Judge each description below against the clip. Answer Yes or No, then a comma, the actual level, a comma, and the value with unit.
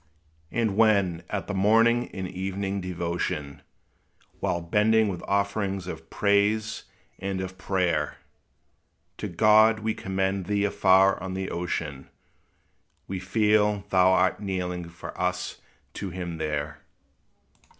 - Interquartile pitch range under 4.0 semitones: Yes, narrow, 2.5 semitones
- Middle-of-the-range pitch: No, very low, 95 Hz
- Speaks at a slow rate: Yes, slow, 120 wpm